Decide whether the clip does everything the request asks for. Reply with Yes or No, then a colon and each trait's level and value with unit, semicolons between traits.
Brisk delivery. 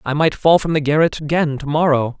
Yes: fast, 245 wpm